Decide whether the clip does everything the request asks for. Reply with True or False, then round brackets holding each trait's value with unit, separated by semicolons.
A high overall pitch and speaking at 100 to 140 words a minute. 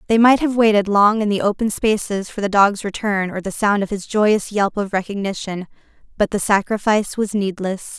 False (205 Hz; 205 wpm)